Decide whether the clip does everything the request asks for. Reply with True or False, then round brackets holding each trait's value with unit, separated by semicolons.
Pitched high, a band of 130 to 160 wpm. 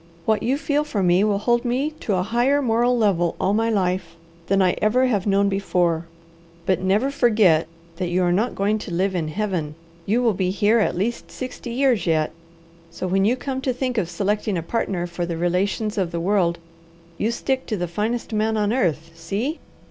False (205 Hz; 205 wpm)